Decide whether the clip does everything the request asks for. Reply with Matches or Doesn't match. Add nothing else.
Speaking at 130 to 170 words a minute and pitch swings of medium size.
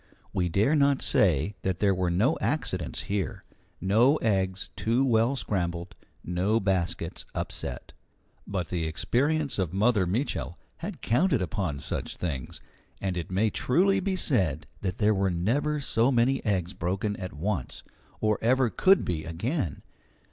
Doesn't match